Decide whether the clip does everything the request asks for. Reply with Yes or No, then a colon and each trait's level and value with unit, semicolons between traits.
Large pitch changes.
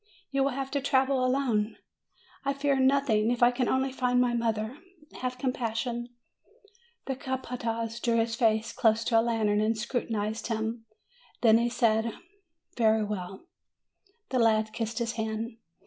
No: narrow, 2.4 semitones